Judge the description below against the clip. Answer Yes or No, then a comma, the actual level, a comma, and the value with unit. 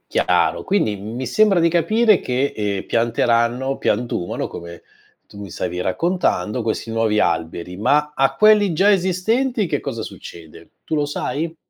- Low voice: Yes, low, 125 Hz